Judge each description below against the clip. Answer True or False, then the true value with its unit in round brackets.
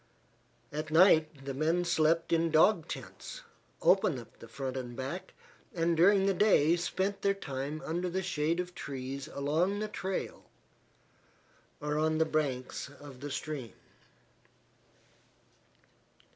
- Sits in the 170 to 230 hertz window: False (155 Hz)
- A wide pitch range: False (4.2 semitones)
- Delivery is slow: True (130 wpm)